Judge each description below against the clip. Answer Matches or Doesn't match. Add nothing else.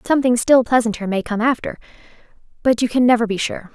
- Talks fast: Doesn't match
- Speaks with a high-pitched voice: Matches